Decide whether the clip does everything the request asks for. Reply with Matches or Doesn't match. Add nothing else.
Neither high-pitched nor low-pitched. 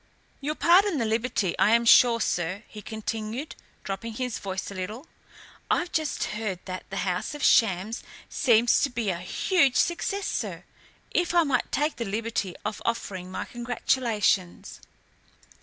Doesn't match